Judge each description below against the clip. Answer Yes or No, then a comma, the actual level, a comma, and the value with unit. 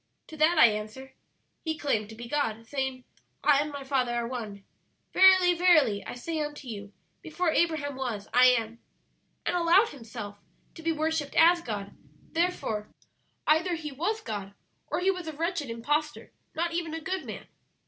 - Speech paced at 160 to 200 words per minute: Yes, average, 170 wpm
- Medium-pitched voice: No, very high, 290 Hz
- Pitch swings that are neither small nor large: No, wide, 6.2 semitones